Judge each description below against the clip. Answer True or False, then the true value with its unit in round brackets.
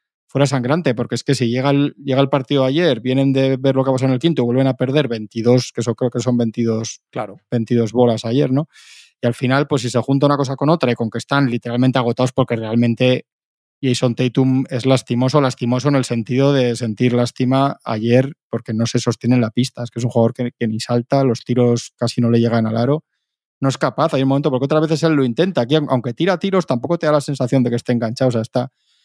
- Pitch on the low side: True (125 Hz)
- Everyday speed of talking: False (250 wpm)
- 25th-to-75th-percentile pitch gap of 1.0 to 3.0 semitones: True (2.4 semitones)